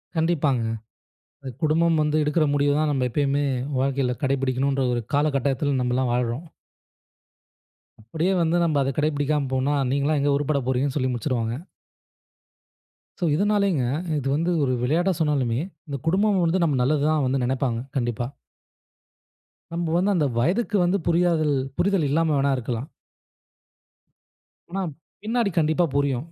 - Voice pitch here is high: No, medium, 145 Hz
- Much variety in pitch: No, average, 3.8 semitones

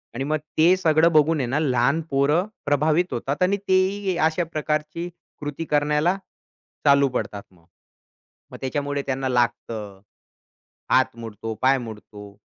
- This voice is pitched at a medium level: Yes, medium, 145 Hz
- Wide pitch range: No, average, 4.3 semitones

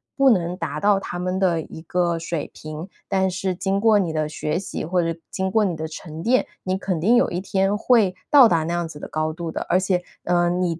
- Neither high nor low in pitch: Yes, medium, 180 Hz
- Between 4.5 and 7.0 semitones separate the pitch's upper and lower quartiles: No, average, 2.7 semitones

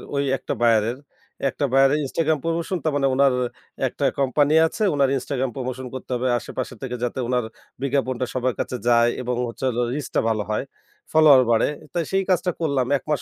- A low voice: Yes, low, 130 Hz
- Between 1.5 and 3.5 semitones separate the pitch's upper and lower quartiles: Yes, average, 2.8 semitones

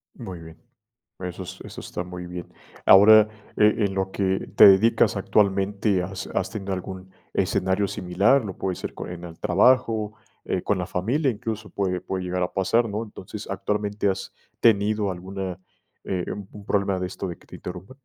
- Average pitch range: No, narrow, 2.3 semitones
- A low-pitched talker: Yes, very low, 95 Hz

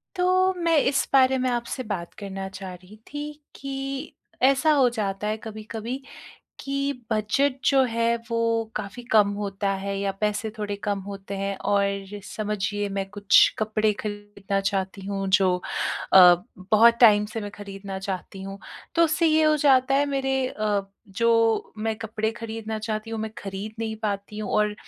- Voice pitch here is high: Yes, high, 215 Hz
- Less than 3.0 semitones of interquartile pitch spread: No, average, 3.6 semitones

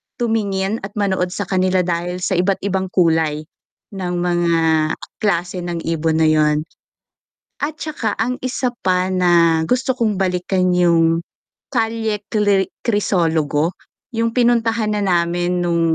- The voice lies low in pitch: No, medium, 185 Hz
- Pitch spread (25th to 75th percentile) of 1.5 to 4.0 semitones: Yes, average, 3.7 semitones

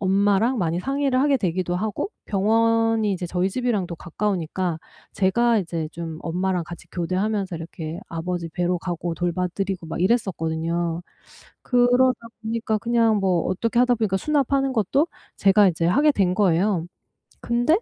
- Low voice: No, high, 190 Hz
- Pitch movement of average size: Yes, average, 4.8 semitones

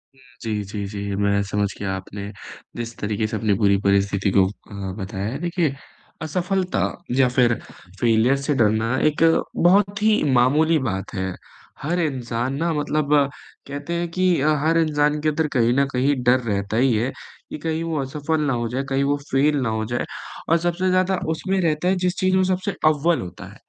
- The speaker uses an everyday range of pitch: No, wide, 7.1 semitones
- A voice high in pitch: No, low, 135 Hz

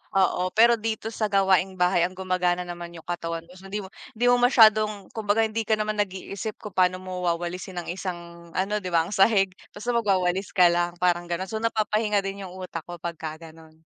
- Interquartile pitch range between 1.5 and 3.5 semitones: Yes, average, 3.2 semitones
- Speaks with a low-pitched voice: No, high, 190 Hz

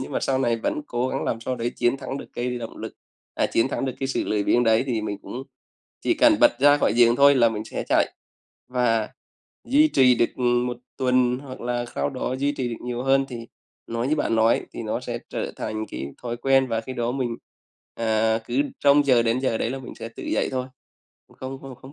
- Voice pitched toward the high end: No, low, 125 Hz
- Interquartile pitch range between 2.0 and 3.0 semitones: Yes, narrow, 2.4 semitones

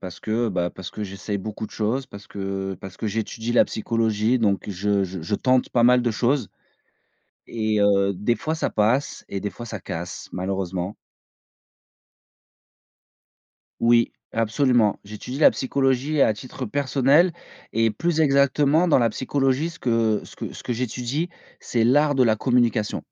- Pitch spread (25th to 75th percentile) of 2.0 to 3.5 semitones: No, average, 4.2 semitones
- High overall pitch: No, low, 115 Hz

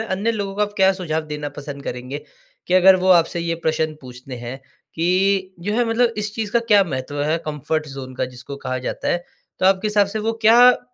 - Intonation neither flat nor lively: No, wide, 5.8 semitones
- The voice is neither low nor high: Yes, medium, 175 Hz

